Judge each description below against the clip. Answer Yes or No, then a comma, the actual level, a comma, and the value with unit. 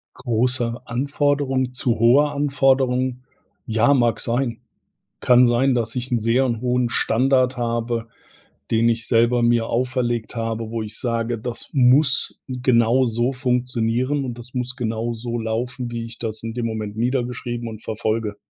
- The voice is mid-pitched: No, low, 120 Hz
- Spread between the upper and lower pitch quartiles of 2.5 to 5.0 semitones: No, narrow, 1.7 semitones